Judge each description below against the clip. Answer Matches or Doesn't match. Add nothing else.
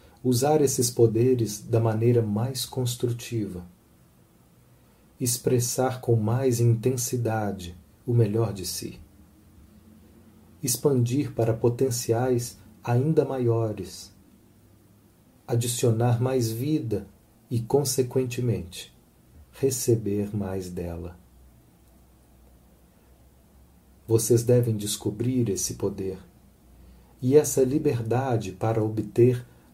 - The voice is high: Doesn't match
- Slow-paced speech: Matches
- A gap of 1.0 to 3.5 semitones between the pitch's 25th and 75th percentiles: Doesn't match